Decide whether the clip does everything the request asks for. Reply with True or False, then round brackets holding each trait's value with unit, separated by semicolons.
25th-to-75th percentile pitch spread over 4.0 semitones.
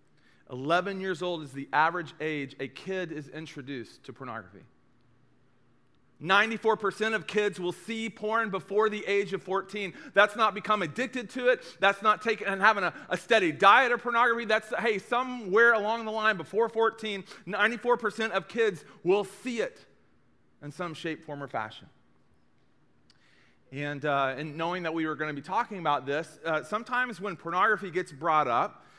True (5.6 semitones)